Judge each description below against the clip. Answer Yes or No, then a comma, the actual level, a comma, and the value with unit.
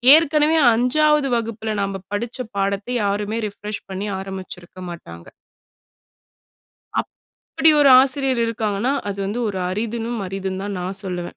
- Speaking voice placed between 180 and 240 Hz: Yes, high, 210 Hz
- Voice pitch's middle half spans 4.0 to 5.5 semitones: Yes, average, 4.3 semitones